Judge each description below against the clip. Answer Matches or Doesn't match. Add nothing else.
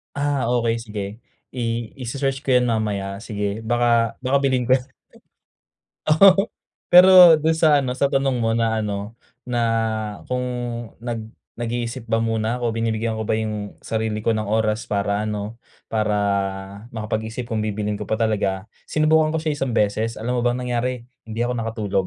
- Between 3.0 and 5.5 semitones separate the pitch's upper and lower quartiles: Doesn't match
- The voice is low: Matches